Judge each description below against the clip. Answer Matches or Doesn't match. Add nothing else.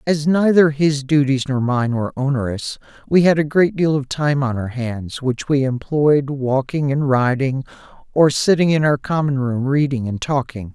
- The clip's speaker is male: Matches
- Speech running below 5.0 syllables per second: Matches